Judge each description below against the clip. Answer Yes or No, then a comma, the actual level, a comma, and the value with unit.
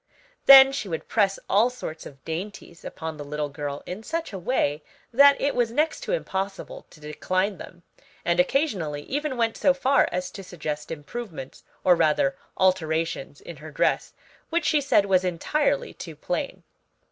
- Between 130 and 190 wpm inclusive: Yes, average, 170 wpm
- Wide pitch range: Yes, wide, 8.6 semitones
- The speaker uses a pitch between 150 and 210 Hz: Yes, medium, 185 Hz